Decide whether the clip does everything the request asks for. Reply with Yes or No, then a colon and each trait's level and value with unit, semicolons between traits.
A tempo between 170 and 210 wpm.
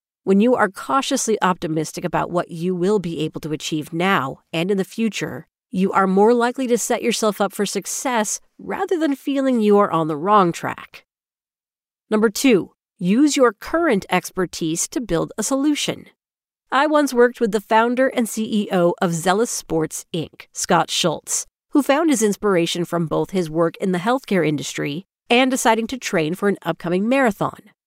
Yes: average, 175 wpm